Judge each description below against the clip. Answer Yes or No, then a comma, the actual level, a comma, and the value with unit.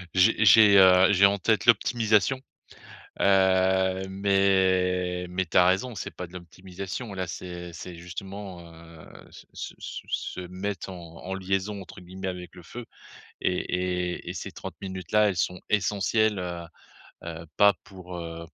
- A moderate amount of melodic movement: No, narrow, 1.7 semitones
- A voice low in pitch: Yes, very low, 95 Hz